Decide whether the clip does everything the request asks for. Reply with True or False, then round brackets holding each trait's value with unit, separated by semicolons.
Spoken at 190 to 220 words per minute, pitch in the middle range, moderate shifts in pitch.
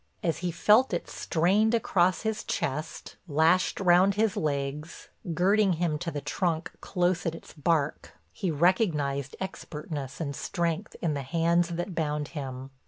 False (150 wpm; 170 Hz; 3.6 semitones)